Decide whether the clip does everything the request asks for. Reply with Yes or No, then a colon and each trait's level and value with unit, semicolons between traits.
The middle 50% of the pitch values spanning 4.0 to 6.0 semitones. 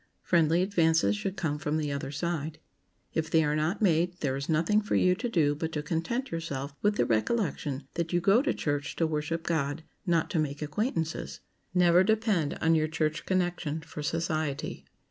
No: average, 2.9 semitones